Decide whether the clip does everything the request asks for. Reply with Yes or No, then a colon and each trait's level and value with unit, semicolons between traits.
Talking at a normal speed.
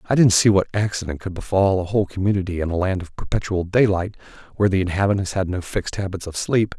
No: fast, 220 wpm